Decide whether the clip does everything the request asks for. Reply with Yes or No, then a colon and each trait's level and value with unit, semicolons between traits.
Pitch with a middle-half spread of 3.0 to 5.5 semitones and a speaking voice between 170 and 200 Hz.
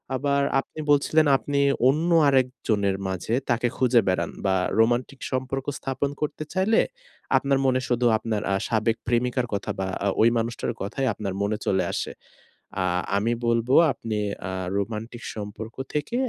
No: average, 3.9 semitones; low, 120 Hz